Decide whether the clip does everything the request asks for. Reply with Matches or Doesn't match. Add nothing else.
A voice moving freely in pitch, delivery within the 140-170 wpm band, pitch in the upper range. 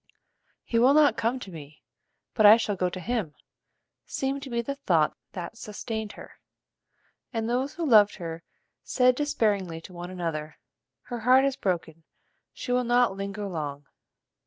Matches